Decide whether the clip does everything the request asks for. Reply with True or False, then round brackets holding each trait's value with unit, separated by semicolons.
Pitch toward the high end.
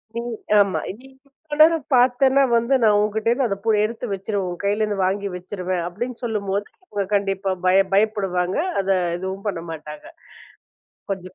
True (200 Hz)